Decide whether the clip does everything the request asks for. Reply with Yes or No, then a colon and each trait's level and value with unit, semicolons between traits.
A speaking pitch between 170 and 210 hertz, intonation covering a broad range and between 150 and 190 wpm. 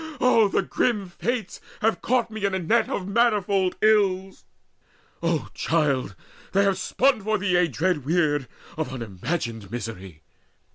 No: medium, 185 Hz; wide, 6.3 semitones; average, 140 wpm